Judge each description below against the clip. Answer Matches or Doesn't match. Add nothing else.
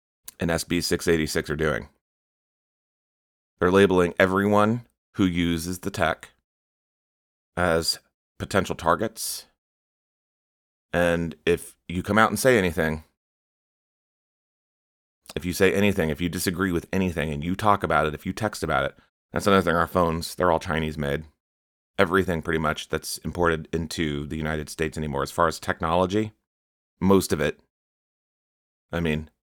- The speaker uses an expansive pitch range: Doesn't match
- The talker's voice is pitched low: Matches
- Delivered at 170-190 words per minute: Doesn't match